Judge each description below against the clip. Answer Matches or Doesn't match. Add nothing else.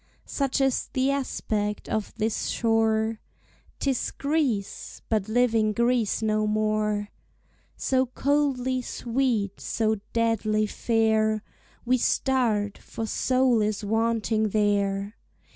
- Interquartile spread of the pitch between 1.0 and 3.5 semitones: Matches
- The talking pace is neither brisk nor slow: Doesn't match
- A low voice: Doesn't match